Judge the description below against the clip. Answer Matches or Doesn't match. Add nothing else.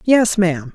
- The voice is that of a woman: Matches